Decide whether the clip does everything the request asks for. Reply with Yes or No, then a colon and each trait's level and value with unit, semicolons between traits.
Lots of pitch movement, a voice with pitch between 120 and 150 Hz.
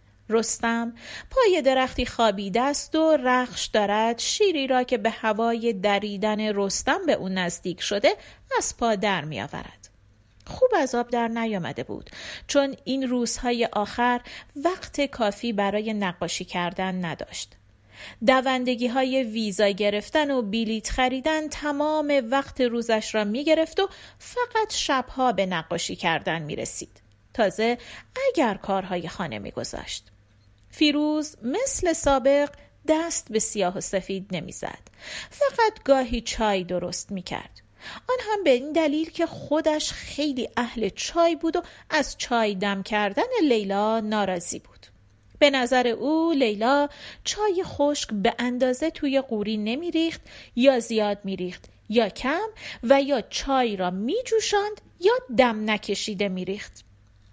No: wide, 6.4 semitones; high, 235 Hz